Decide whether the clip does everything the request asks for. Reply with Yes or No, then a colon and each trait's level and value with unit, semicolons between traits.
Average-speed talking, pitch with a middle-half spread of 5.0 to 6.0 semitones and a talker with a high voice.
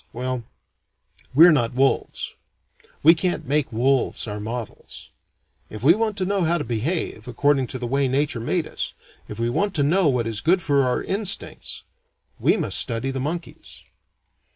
No: average, 170 wpm; wide, 5.5 semitones; low, 135 Hz